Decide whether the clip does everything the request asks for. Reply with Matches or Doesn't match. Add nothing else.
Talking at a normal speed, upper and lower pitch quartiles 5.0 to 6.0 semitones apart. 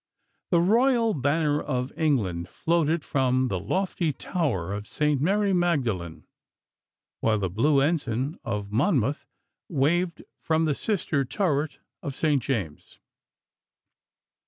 Doesn't match